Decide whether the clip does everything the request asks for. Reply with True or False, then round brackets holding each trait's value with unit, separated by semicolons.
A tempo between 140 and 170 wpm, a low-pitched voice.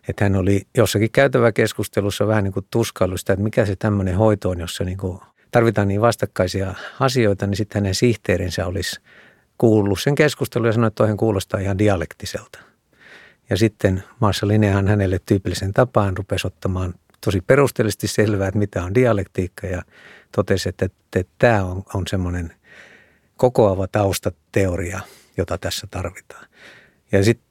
True (150 wpm; 100 Hz)